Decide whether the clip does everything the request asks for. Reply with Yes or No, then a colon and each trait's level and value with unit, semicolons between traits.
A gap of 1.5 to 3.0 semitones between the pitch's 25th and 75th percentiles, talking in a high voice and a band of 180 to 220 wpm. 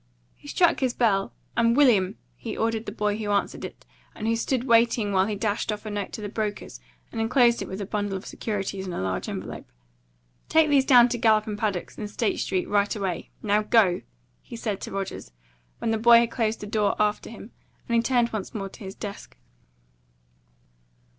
Yes: narrow, 2.5 semitones; high, 215 Hz; fast, 205 wpm